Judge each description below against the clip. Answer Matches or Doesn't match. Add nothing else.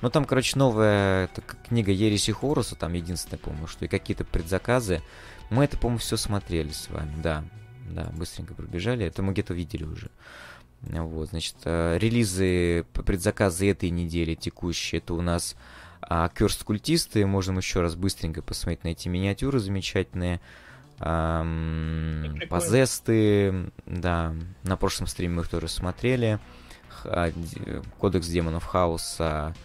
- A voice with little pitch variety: Doesn't match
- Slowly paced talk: Doesn't match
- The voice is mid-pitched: Doesn't match